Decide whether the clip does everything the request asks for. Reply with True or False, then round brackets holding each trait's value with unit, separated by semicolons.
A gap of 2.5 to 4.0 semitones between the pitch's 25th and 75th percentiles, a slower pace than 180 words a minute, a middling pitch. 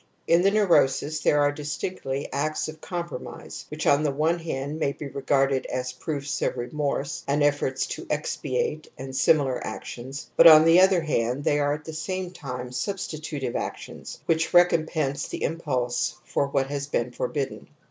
True (2.9 semitones; 170 wpm; 145 Hz)